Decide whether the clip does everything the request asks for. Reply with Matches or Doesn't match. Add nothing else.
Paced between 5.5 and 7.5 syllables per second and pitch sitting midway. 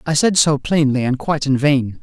Doesn't match